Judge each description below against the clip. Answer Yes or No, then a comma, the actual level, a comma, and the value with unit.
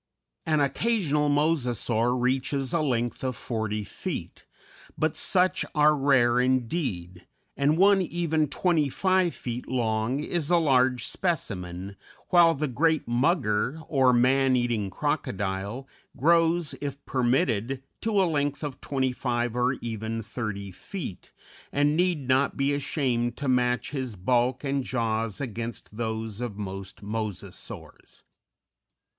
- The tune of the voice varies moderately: Yes, average, 4.6 semitones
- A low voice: Yes, low, 130 Hz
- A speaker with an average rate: No, slow, 125 wpm